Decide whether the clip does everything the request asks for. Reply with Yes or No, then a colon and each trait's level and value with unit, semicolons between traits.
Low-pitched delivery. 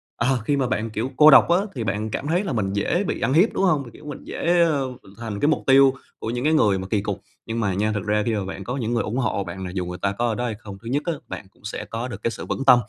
Yes: low, 115 Hz